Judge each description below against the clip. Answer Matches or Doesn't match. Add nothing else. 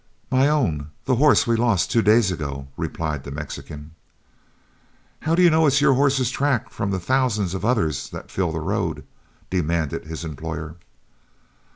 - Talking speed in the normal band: Matches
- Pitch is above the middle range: Doesn't match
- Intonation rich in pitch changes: Matches